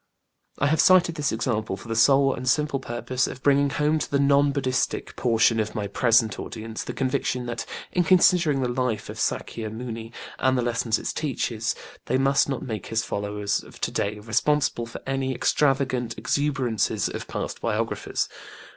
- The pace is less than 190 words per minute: Yes, average, 175 wpm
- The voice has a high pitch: No, low, 125 Hz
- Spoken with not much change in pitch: No, average, 3.6 semitones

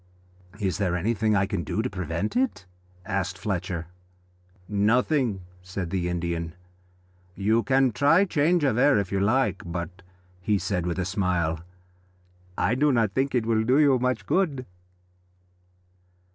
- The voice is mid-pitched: No, low, 105 Hz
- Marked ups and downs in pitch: Yes, wide, 5.8 semitones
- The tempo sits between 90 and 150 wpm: Yes, average, 145 wpm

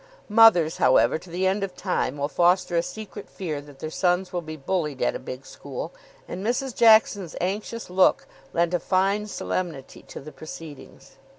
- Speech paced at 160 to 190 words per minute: Yes, average, 180 wpm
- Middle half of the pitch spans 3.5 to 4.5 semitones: Yes, average, 4.0 semitones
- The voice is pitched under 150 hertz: No, medium, 180 Hz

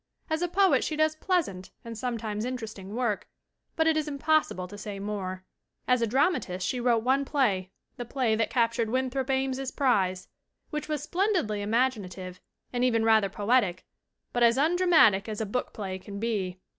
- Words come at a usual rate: Yes, average, 170 wpm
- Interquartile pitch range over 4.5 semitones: Yes, average, 4.9 semitones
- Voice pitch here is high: Yes, high, 235 Hz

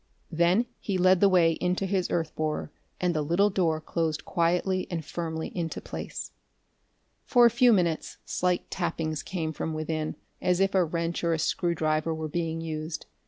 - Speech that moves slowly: No, average, 170 wpm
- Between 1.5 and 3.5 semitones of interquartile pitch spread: Yes, narrow, 2.4 semitones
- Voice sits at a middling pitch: Yes, medium, 170 Hz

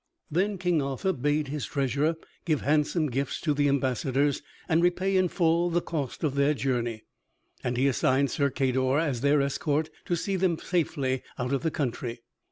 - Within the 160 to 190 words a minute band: Yes, average, 175 wpm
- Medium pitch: Yes, medium, 145 Hz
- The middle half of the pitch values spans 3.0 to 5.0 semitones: Yes, average, 3.8 semitones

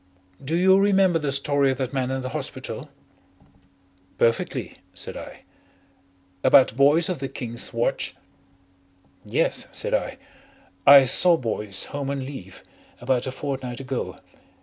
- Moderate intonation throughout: No, narrow, 2.3 semitones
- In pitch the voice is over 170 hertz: No, low, 135 Hz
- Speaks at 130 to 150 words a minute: Yes, slow, 135 wpm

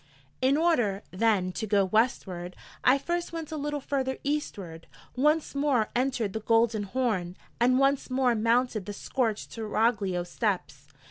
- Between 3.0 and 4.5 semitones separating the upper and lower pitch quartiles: No, average, 5.2 semitones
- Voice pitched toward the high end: Yes, high, 230 Hz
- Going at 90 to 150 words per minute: Yes, average, 145 wpm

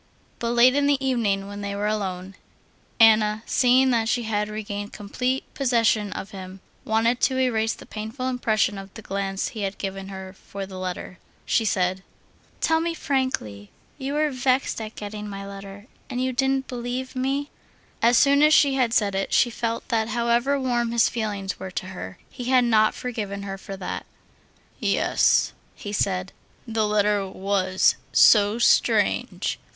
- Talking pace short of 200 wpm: Yes, average, 170 wpm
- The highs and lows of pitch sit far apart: No, average, 4.0 semitones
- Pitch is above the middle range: Yes, high, 220 Hz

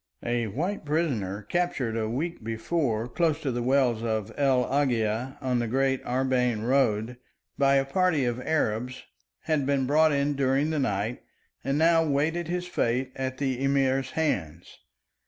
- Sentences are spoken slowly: No, average, 155 wpm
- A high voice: No, low, 135 Hz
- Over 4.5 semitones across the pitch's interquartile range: No, average, 3.6 semitones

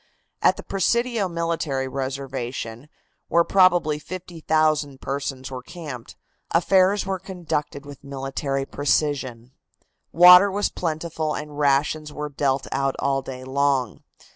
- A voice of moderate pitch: Yes, medium, 145 Hz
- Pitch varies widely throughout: No, average, 3.9 semitones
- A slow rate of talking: Yes, slow, 115 wpm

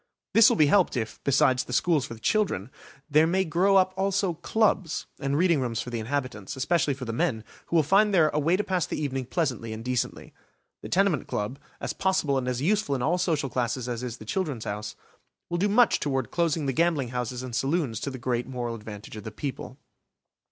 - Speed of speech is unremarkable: No, fast, 220 wpm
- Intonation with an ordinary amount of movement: No, wide, 6.0 semitones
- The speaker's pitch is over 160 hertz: No, medium, 140 Hz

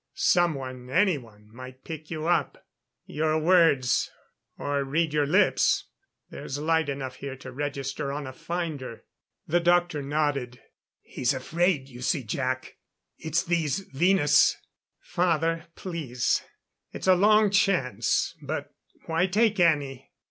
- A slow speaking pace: Yes, slow, 125 wpm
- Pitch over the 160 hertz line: No, medium, 150 Hz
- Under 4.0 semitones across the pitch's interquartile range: No, average, 4.6 semitones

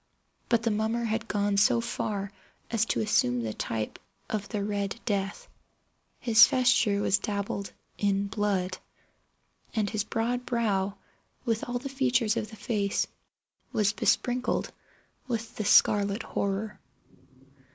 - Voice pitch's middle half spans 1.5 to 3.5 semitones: Yes, narrow, 2.5 semitones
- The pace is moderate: No, slow, 130 wpm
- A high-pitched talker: Yes, high, 215 Hz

